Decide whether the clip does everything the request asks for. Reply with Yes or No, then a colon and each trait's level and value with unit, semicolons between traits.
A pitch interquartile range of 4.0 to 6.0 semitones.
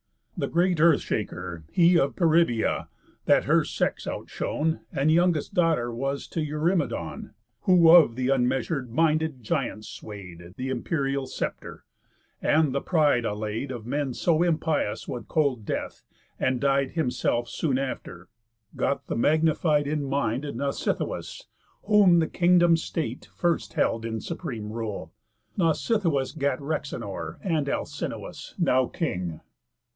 Yes: average, 5.3 semitones